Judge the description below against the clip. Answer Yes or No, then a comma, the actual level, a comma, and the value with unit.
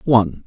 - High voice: No, low, 120 Hz